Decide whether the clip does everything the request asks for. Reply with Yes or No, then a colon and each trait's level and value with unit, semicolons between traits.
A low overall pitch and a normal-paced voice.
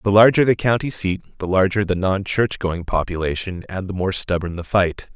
No: very low, 95 Hz; fast, 210 wpm